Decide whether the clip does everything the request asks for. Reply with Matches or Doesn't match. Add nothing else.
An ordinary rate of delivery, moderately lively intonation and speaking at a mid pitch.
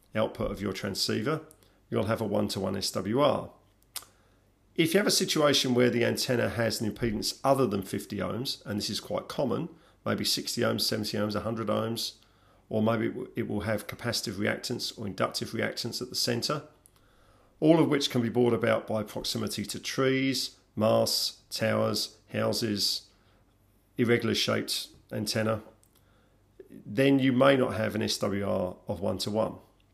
Doesn't match